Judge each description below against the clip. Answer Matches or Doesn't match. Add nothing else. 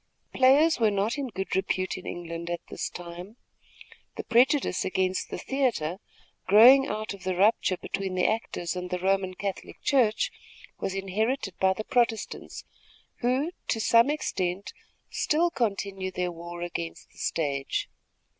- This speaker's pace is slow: Doesn't match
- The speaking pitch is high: Matches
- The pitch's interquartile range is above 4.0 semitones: Matches